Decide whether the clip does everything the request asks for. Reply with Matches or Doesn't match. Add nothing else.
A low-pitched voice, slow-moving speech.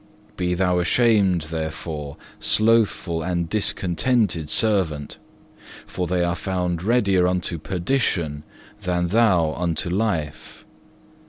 Matches